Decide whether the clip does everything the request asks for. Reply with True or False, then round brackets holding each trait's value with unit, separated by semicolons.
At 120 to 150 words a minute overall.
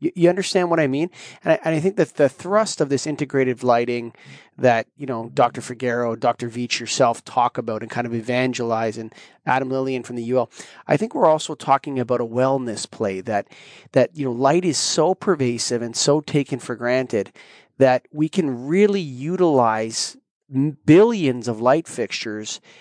False (180 wpm)